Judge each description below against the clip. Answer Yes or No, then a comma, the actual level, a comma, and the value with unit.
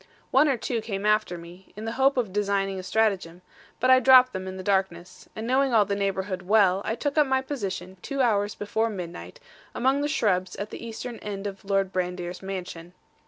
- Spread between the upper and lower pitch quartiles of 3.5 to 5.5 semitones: Yes, average, 4.2 semitones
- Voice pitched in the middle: No, high, 205 Hz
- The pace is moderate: No, fast, 210 wpm